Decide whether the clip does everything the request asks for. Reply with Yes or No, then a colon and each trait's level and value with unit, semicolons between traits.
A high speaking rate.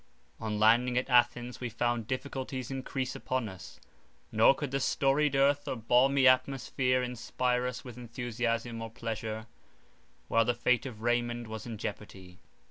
No: average, 150 wpm